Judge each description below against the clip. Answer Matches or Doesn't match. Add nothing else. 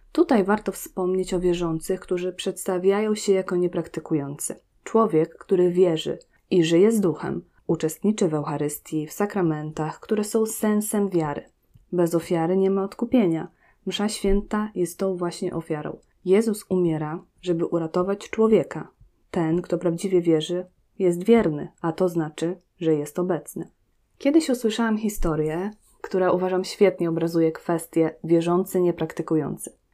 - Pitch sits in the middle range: Matches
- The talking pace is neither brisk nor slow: Matches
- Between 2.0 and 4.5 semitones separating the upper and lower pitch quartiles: Matches